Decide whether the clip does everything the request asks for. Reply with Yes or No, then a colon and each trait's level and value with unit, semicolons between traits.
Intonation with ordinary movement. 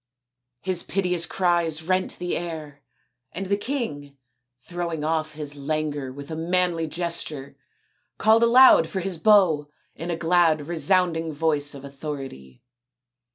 Yes: average, 3.3 semitones